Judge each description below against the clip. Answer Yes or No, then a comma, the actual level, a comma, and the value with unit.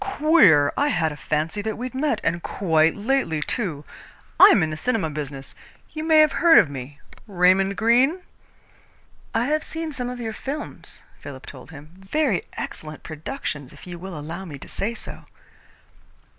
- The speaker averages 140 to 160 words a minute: No, average, 170 wpm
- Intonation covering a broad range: Yes, wide, 8.8 semitones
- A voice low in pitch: No, high, 190 Hz